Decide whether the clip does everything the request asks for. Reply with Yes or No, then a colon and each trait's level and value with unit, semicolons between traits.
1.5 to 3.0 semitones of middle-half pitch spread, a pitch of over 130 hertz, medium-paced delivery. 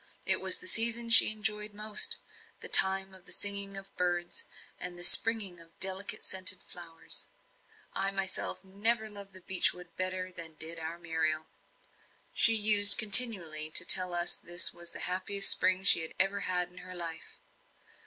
Yes: narrow, 2.6 semitones; high, 190 Hz; average, 170 wpm